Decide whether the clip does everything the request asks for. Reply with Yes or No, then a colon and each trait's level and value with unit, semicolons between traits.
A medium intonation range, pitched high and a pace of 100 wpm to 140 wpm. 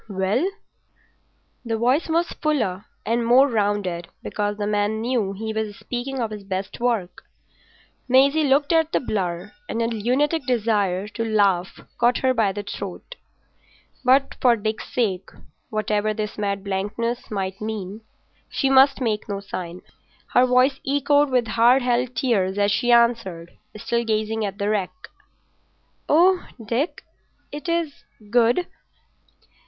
Yes: average, 4.0 semitones; high, 225 Hz; slow, 135 wpm